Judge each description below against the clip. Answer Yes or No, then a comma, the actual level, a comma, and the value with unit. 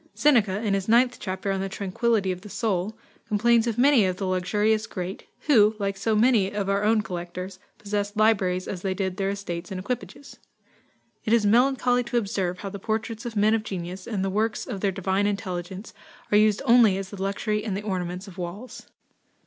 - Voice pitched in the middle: No, high, 205 Hz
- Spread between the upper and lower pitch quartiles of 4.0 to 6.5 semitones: No, average, 2.8 semitones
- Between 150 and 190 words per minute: No, average, 200 wpm